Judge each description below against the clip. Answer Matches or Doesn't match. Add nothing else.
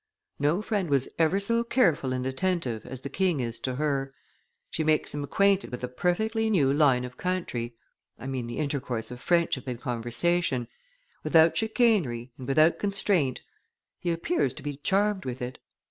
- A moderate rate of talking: Matches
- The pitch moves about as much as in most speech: Doesn't match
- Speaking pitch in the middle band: Matches